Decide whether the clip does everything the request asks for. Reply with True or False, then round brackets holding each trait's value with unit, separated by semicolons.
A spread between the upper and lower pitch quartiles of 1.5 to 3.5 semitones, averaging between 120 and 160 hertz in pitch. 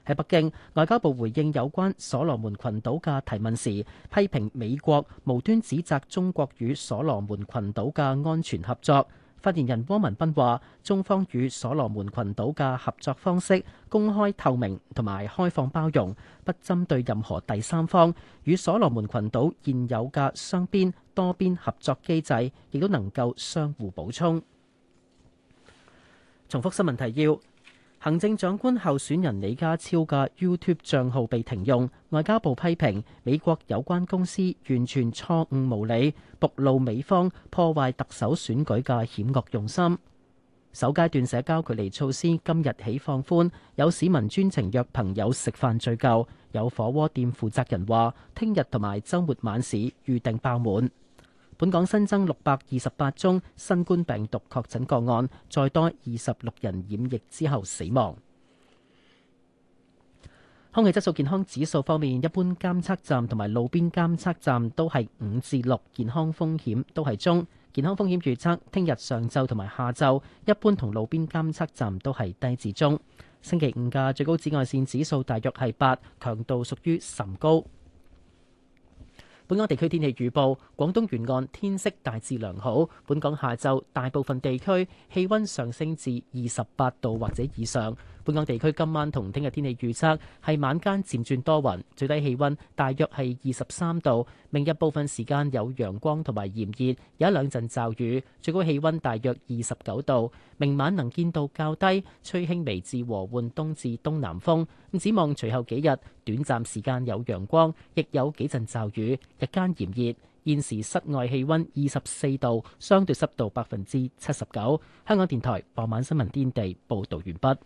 False (5.3 semitones; 135 Hz)